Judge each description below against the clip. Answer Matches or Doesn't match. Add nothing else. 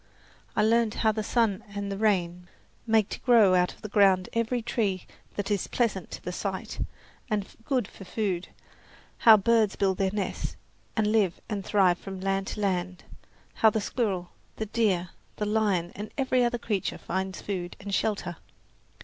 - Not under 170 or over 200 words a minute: Matches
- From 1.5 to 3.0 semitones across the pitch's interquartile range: Matches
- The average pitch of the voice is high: Matches